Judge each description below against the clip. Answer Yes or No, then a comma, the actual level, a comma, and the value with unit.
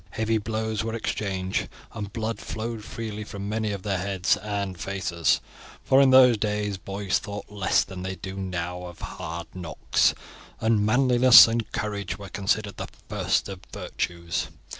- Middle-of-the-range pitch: No, low, 105 Hz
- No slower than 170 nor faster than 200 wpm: No, average, 160 wpm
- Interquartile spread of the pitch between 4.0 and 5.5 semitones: No, average, 2.7 semitones